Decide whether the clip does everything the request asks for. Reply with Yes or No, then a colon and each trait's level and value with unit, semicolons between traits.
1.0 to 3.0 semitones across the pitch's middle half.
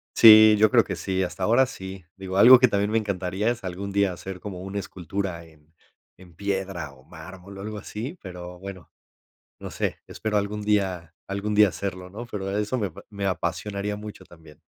Yes: narrow, 2.4 semitones